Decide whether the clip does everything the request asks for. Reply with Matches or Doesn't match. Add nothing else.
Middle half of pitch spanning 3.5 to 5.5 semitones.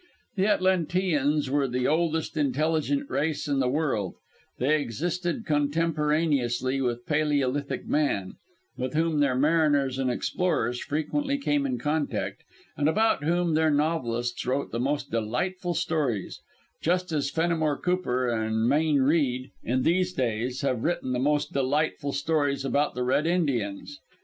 Matches